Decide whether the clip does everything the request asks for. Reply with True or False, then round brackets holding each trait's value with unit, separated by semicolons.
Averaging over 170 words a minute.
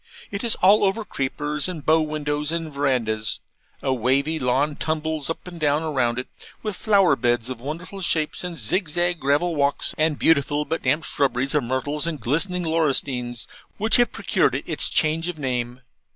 True (180 wpm)